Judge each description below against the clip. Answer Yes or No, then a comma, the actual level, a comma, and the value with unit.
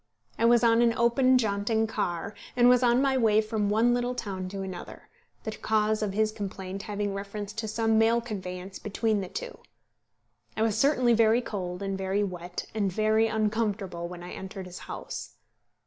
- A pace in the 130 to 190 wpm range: Yes, average, 180 wpm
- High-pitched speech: Yes, high, 215 Hz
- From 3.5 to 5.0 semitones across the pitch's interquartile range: No, average, 2.8 semitones